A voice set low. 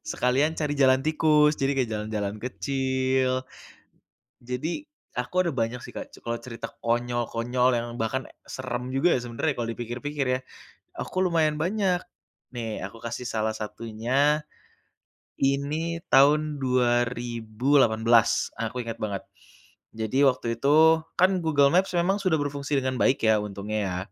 Yes: low, 130 Hz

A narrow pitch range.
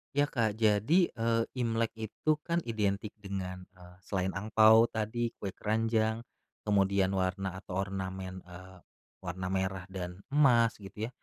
No: average, 3.3 semitones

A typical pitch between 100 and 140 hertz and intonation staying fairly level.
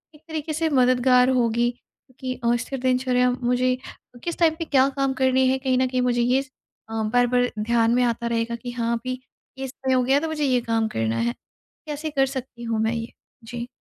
No: very high, 250 Hz; narrow, 2.0 semitones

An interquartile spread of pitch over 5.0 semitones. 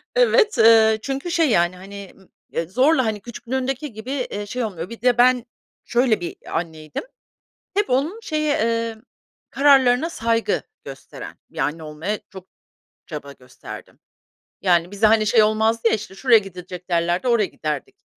Yes: wide, 5.6 semitones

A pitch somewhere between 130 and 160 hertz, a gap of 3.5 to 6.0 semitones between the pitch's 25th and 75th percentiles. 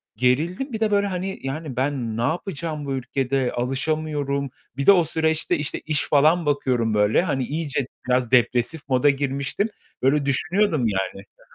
Yes: medium, 140 Hz; average, 3.9 semitones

